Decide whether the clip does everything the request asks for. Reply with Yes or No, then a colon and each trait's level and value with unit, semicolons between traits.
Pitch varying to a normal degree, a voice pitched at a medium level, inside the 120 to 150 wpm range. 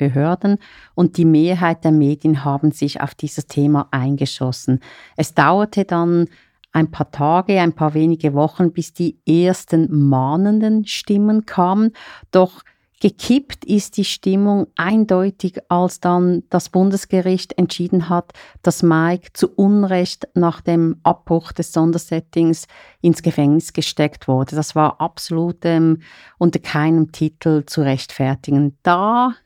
Yes: average, 3.3 semitones; medium, 170 Hz; average, 130 wpm